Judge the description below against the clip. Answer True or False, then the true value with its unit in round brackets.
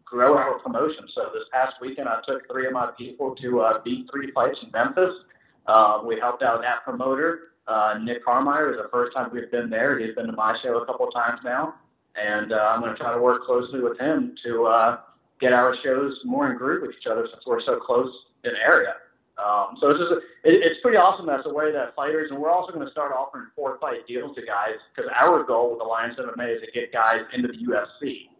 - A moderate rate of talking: False (240 wpm)